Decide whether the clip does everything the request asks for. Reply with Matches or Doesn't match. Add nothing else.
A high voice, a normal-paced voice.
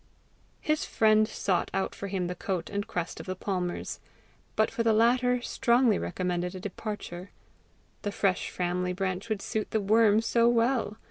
Matches